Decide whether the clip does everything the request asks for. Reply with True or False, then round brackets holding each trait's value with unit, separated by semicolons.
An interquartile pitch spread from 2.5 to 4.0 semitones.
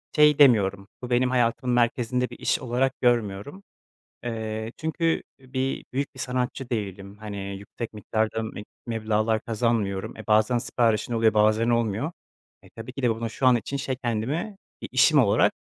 True (2.8 semitones)